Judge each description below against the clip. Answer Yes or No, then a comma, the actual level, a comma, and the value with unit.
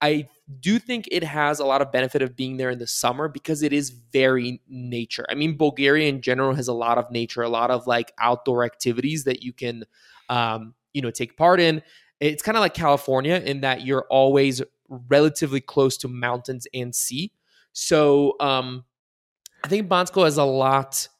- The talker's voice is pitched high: No, low, 135 Hz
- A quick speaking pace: No, average, 190 wpm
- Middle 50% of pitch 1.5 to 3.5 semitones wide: Yes, average, 3.1 semitones